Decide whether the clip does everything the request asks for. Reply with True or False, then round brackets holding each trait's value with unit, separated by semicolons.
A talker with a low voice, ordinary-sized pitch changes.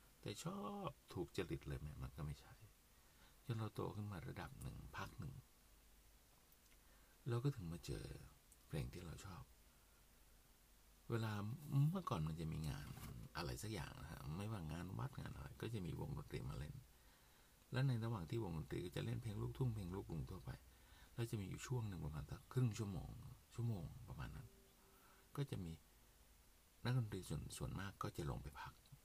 False (105 Hz; 7.4 semitones)